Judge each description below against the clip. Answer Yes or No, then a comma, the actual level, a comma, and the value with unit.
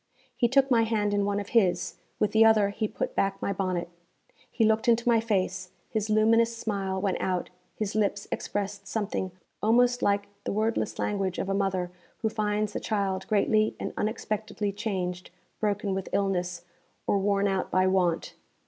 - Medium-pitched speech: No, high, 205 Hz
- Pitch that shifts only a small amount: Yes, narrow, 2.3 semitones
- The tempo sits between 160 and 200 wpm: Yes, average, 175 wpm